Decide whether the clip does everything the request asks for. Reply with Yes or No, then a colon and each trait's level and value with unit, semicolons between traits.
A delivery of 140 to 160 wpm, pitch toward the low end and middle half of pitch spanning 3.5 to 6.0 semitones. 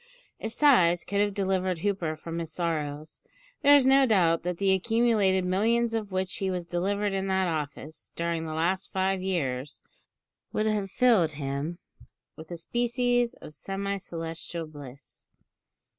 No: average, 155 wpm; medium, 185 Hz; average, 3.9 semitones